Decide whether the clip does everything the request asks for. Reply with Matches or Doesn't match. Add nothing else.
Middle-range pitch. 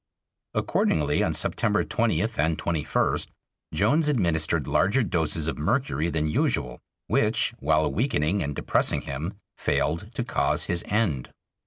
Doesn't match